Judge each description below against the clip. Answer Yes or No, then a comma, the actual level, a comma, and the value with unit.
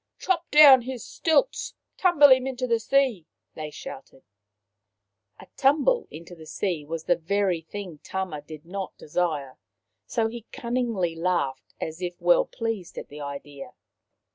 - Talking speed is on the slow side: No, average, 155 wpm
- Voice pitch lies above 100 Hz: Yes, high, 190 Hz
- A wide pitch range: Yes, wide, 8.1 semitones